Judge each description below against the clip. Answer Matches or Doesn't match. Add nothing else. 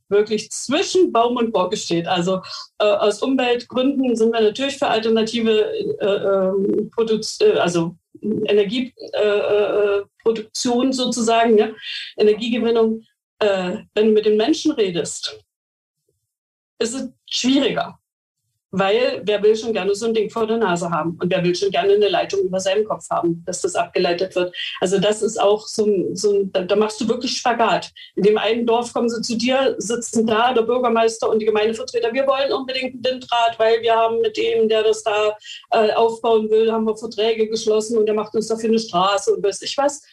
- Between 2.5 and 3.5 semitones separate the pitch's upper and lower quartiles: Matches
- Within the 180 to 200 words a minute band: Matches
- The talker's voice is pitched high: Matches